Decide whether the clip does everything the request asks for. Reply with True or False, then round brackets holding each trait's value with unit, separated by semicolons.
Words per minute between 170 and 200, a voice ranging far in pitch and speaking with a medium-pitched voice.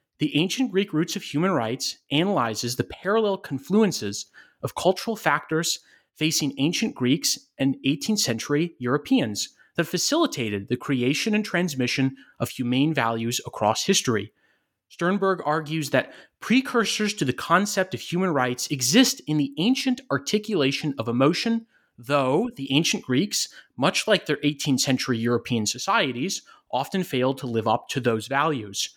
False (140 wpm; 7.3 semitones; 150 Hz)